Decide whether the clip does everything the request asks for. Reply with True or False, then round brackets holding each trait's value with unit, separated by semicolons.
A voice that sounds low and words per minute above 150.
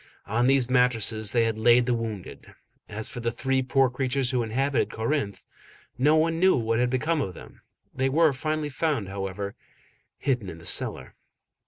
True (125 Hz; 175 wpm)